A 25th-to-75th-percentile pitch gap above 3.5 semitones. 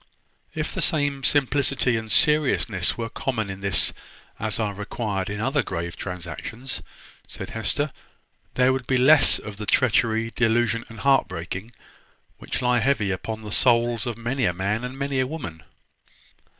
Yes: average, 4.3 semitones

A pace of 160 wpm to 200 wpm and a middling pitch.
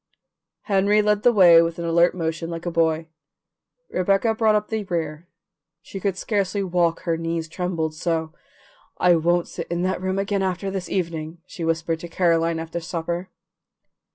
Yes: average, 165 wpm; medium, 175 Hz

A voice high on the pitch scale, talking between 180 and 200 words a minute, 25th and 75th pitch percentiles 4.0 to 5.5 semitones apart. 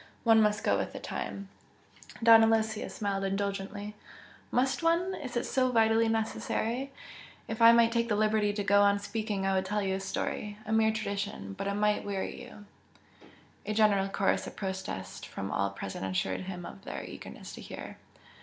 No: high, 210 Hz; average, 190 wpm; narrow, 2.4 semitones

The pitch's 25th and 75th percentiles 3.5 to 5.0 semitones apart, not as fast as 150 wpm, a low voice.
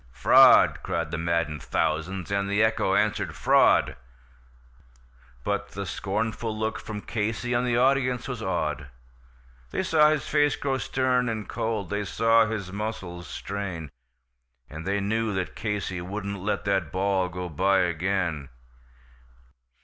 Yes: average, 3.9 semitones; average, 140 wpm; low, 100 Hz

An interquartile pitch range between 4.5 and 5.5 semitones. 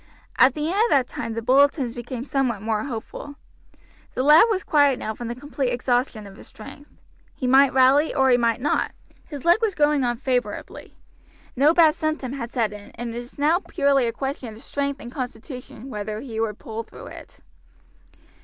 No: average, 3.5 semitones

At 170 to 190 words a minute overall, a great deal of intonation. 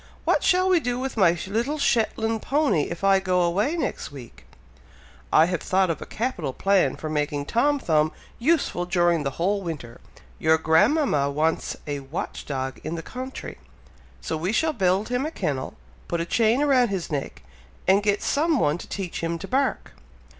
Yes: average, 180 wpm; wide, 7.7 semitones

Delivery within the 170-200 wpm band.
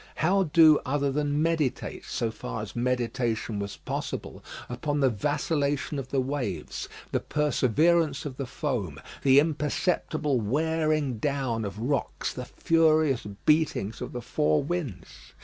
No: slow, 135 wpm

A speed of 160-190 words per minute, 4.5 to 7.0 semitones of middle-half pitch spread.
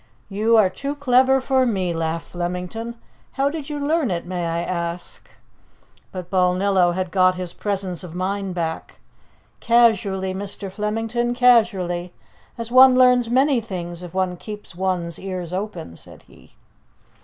No: average, 145 wpm; average, 4.9 semitones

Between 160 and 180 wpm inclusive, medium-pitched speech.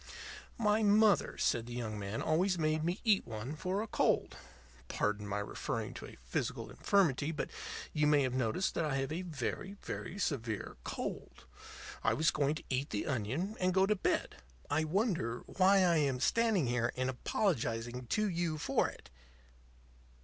Yes: average, 170 wpm; medium, 155 Hz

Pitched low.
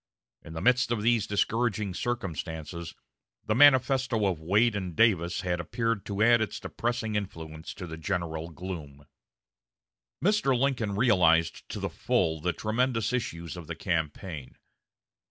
Yes: low, 100 Hz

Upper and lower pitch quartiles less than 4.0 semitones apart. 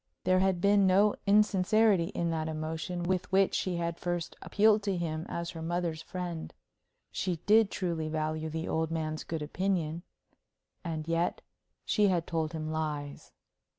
Yes: average, 2.9 semitones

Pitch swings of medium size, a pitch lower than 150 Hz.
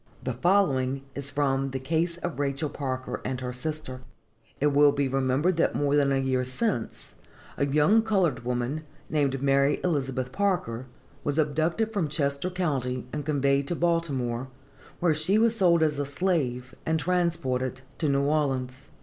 Yes: average, 3.9 semitones; medium, 140 Hz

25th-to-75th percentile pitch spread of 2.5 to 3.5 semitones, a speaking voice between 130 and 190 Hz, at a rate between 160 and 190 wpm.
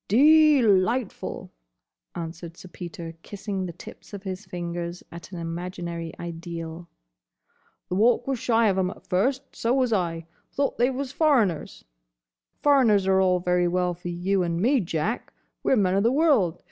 No: wide, 5.4 semitones; medium, 185 Hz; average, 165 wpm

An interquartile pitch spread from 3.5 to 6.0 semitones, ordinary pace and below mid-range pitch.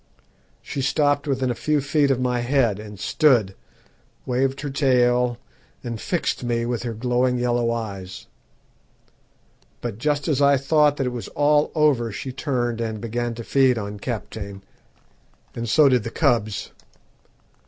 No: average, 3.0 semitones; average, 155 wpm; low, 125 Hz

